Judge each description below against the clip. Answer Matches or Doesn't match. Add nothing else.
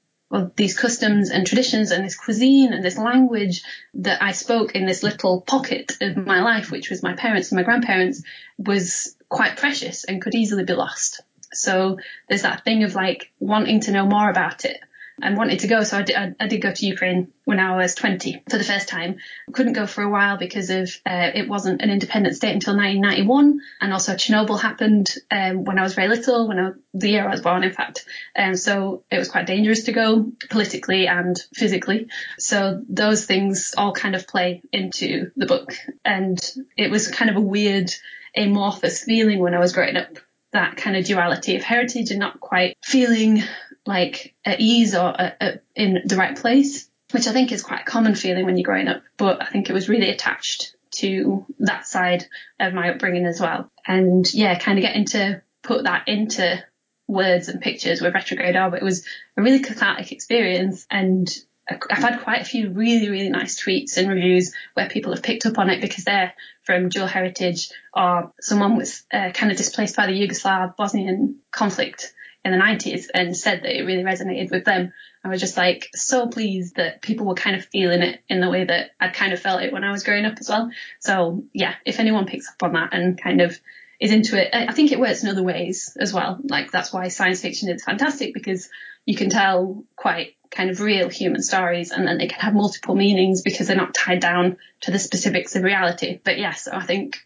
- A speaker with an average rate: Doesn't match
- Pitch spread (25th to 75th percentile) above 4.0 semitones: Doesn't match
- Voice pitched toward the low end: Doesn't match